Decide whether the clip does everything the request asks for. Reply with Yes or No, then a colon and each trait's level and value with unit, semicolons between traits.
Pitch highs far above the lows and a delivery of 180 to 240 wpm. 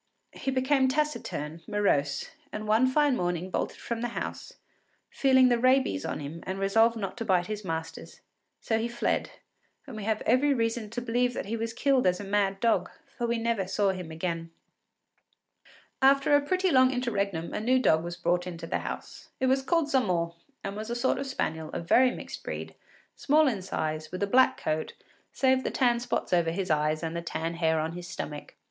Yes: wide, 6.8 semitones; average, 200 wpm